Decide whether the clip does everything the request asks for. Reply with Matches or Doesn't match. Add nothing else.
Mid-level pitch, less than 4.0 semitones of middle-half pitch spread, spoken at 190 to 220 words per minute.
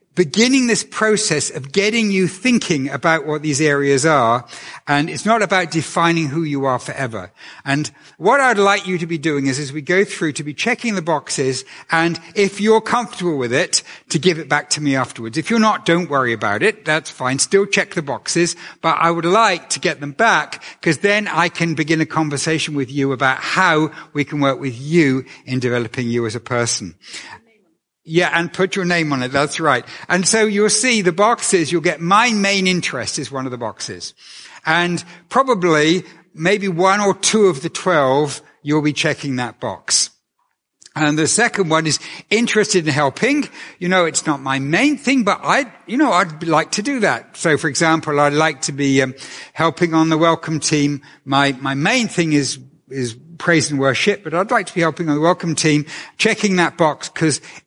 Doesn't match